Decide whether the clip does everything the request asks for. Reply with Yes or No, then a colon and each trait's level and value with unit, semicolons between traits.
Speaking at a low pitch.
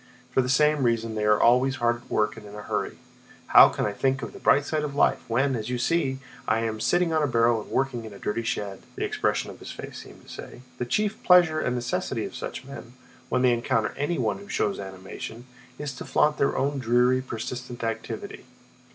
Yes: low, 125 Hz